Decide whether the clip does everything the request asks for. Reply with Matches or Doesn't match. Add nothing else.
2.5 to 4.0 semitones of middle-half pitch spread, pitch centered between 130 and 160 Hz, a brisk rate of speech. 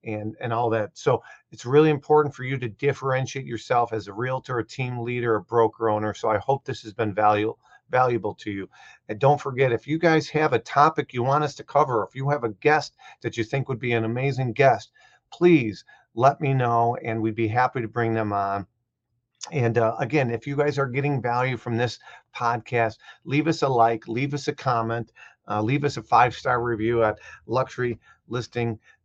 Doesn't match